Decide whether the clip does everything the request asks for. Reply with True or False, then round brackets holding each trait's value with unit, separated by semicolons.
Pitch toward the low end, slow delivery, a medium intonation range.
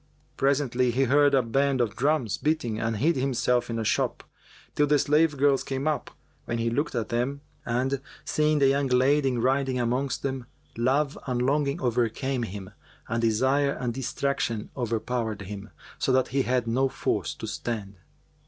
False (130 Hz; 170 wpm; 3.0 semitones)